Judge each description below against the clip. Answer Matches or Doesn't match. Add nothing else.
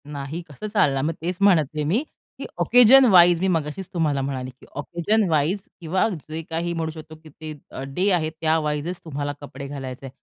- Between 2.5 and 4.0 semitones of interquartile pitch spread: Matches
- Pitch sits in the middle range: Matches